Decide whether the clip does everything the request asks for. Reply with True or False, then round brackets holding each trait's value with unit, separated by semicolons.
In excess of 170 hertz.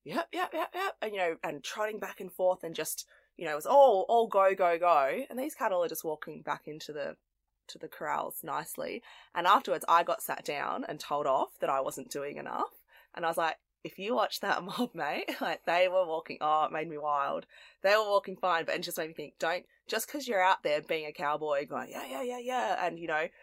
True (185 Hz)